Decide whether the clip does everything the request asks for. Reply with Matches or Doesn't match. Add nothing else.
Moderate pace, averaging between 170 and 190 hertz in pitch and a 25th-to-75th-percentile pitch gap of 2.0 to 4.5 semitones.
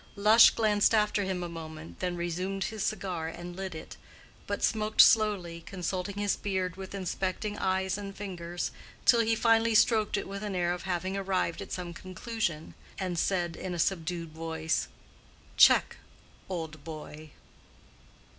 Matches